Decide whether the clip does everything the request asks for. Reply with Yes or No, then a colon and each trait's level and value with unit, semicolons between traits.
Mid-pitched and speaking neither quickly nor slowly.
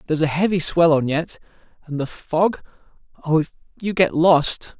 Yes: medium, 160 Hz; average, 150 wpm